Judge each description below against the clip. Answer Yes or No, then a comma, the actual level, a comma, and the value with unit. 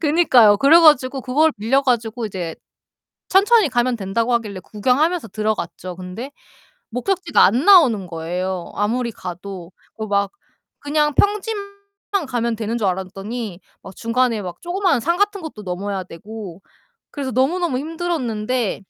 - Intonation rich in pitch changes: Yes, wide, 6.8 semitones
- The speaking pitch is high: Yes, high, 235 Hz